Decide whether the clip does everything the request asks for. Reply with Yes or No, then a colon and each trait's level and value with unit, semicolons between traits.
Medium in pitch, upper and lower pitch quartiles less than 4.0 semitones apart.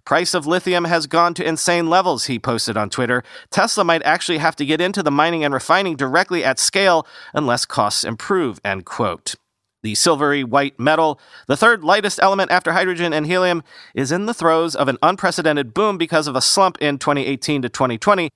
No: medium, 160 Hz; average, 4.3 semitones